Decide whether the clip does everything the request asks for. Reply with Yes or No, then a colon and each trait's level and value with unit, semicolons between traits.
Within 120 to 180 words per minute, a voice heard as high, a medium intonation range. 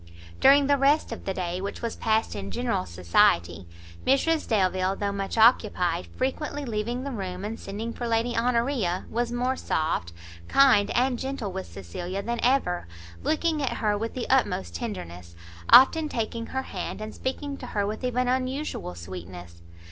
No: average, 165 wpm; high, 225 Hz; wide, 6.0 semitones